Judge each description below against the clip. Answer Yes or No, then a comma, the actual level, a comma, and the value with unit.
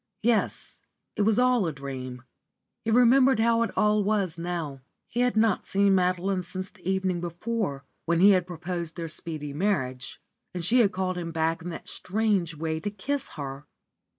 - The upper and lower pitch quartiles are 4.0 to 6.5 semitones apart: Yes, average, 4.5 semitones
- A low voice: No, medium, 185 Hz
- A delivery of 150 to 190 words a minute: Yes, average, 180 wpm